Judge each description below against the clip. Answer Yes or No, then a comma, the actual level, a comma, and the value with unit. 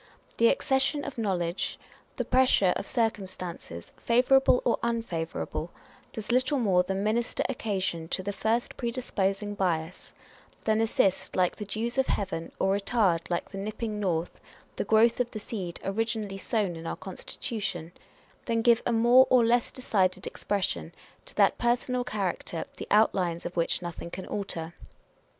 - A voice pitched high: Yes, high, 205 Hz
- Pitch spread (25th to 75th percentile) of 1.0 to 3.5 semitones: No, average, 4.3 semitones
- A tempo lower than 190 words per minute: Yes, average, 155 wpm